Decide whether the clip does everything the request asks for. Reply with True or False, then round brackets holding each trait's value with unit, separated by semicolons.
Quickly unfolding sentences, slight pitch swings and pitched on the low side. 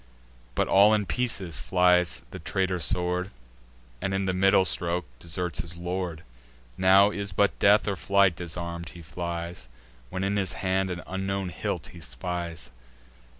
False (150 wpm; 2.1 semitones; 90 Hz)